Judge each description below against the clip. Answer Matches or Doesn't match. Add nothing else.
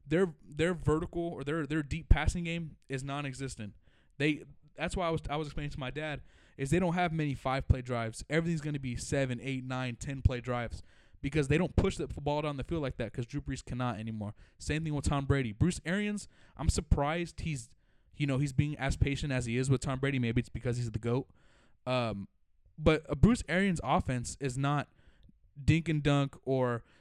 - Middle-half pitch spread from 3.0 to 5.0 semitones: Matches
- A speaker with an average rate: Doesn't match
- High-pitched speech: Doesn't match